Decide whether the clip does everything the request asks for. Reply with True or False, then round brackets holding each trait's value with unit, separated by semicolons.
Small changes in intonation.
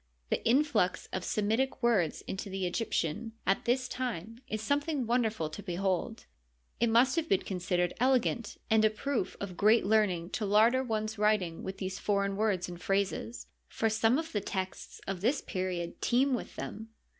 False (3.9 semitones)